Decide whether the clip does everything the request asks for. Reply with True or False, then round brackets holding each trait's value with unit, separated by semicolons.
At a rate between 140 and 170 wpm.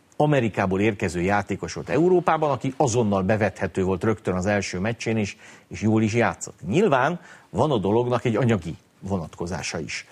True (155 wpm)